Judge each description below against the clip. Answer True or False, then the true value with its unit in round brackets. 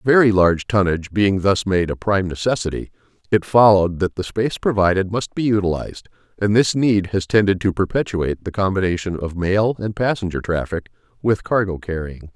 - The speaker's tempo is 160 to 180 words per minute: True (170 wpm)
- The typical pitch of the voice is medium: False (100 Hz)